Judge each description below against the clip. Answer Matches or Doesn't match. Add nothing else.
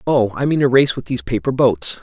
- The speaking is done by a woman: Doesn't match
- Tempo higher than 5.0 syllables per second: Matches